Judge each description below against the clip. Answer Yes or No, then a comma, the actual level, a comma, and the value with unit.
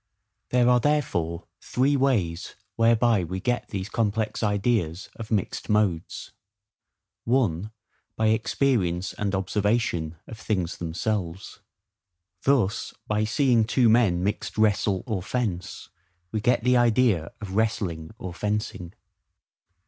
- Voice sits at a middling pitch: No, low, 105 Hz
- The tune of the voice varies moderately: Yes, average, 4.1 semitones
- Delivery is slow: Yes, slow, 115 wpm